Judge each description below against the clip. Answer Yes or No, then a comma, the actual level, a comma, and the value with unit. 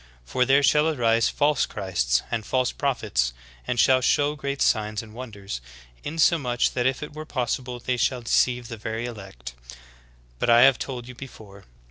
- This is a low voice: Yes, low, 120 Hz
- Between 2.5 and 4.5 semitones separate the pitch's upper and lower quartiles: Yes, average, 3.4 semitones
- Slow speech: No, average, 170 wpm